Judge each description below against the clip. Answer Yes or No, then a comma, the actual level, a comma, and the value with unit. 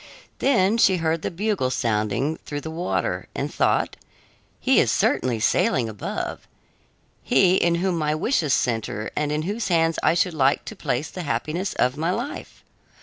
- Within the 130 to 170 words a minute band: Yes, average, 165 wpm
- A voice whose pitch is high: No, medium, 160 Hz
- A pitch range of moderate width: No, wide, 5.7 semitones